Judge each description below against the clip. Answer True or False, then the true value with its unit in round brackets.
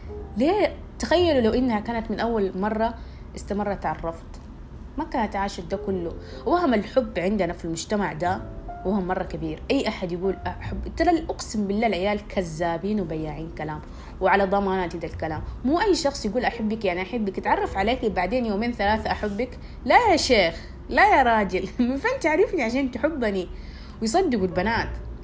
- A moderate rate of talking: False (155 wpm)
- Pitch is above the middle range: True (205 Hz)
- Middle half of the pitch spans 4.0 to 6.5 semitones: True (4.5 semitones)